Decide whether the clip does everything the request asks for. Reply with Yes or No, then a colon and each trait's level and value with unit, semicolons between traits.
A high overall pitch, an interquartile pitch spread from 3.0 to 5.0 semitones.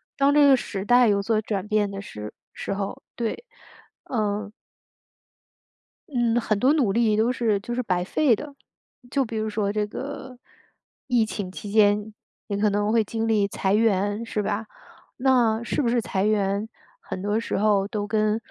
No: high, 215 Hz; narrow, 2.6 semitones